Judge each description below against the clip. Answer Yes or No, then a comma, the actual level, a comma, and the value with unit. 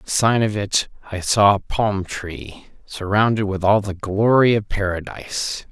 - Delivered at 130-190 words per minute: Yes, average, 170 wpm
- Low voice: Yes, low, 100 Hz